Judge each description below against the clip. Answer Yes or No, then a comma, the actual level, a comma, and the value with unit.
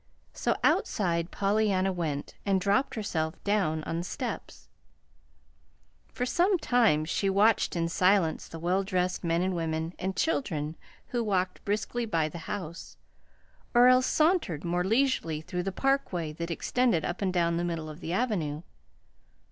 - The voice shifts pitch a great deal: No, average, 4.2 semitones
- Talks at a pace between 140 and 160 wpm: Yes, average, 150 wpm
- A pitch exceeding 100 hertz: Yes, medium, 185 Hz